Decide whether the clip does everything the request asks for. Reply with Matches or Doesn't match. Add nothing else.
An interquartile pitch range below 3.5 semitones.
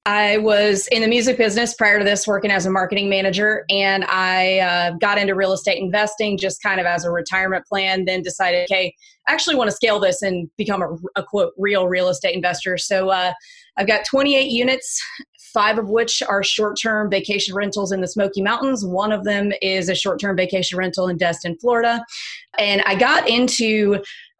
Matches